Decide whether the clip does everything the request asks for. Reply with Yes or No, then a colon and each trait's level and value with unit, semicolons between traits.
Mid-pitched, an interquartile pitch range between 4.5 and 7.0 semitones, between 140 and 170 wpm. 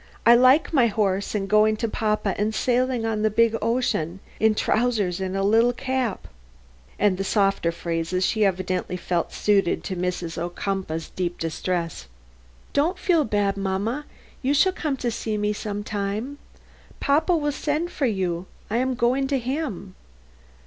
No: high, 215 Hz; average, 5.0 semitones; average, 160 wpm